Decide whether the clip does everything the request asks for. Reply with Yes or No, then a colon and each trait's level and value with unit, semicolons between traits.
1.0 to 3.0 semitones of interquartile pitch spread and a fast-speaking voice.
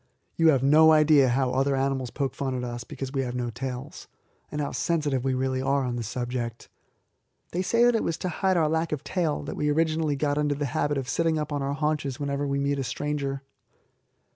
Yes: narrow, 2.5 semitones; fast, 225 wpm